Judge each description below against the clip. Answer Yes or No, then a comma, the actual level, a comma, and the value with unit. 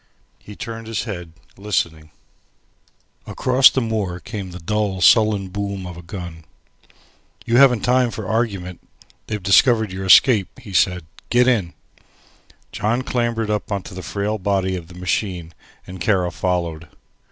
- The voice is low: Yes, low, 100 Hz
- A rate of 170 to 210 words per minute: No, average, 145 wpm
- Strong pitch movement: No, average, 3.7 semitones